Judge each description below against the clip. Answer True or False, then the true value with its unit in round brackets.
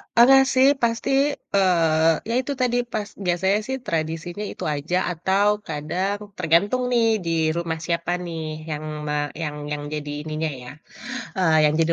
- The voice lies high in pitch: False (170 Hz)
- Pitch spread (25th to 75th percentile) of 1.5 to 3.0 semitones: False (4.4 semitones)